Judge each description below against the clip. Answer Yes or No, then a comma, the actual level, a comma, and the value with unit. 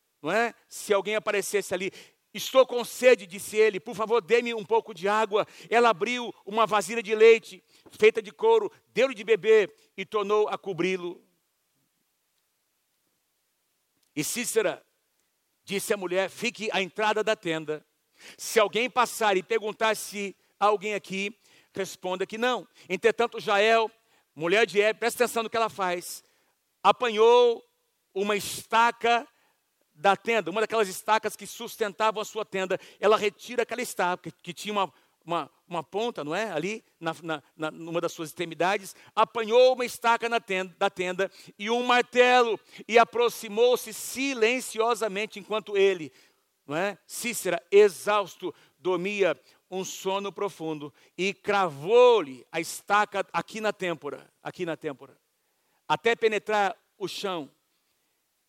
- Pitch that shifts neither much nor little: Yes, average, 3.6 semitones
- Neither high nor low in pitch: No, high, 210 Hz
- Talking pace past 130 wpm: Yes, average, 140 wpm